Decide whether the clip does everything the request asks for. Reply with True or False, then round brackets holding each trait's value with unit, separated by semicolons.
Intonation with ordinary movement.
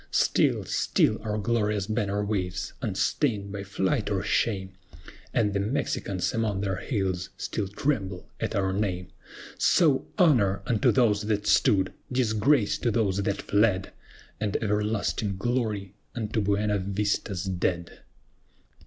False (2.3 semitones)